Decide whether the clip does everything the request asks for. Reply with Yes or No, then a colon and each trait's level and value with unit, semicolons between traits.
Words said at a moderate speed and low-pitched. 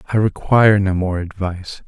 Yes: average, 160 wpm; very low, 95 Hz